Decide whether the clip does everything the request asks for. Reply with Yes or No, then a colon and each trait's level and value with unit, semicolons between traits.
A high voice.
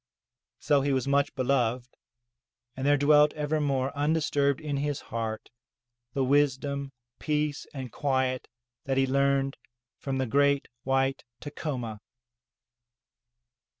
No: medium, 140 Hz